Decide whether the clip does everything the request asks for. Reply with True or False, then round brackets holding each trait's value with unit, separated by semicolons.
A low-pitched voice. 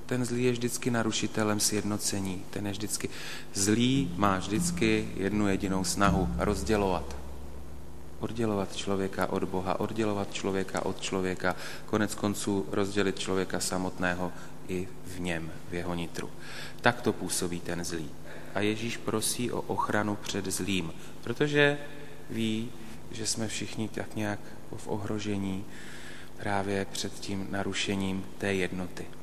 True (100 Hz)